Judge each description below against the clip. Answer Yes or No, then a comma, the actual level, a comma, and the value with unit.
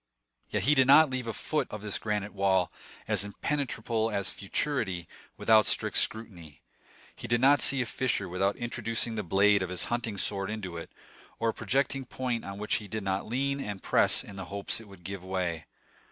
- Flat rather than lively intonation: No, average, 3.7 semitones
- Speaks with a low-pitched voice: Yes, low, 105 Hz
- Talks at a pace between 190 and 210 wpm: Yes, average, 195 wpm